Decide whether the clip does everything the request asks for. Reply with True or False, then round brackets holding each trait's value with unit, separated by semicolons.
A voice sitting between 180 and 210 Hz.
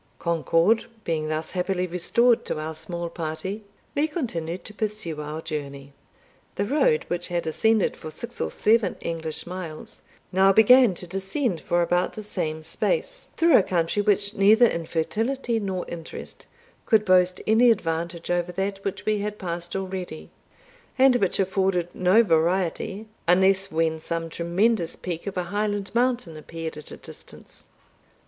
True (185 Hz)